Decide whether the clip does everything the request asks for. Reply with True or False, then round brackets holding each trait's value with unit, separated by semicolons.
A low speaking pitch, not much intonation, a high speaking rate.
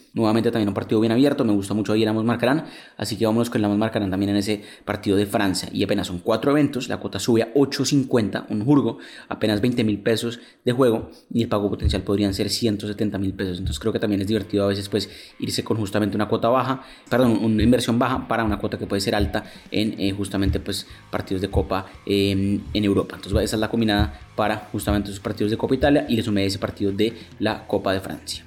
True (105 Hz; 2.3 semitones; 230 wpm)